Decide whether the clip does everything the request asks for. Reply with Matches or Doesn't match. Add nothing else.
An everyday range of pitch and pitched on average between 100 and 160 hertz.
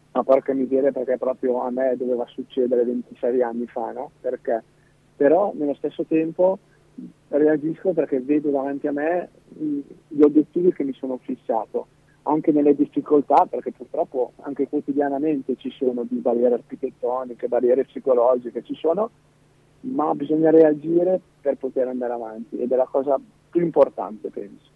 Matches